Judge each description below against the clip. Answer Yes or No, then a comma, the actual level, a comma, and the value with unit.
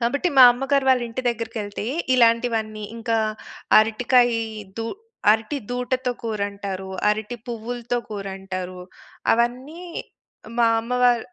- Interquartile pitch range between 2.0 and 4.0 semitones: Yes, narrow, 2.5 semitones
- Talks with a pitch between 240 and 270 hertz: No, high, 230 Hz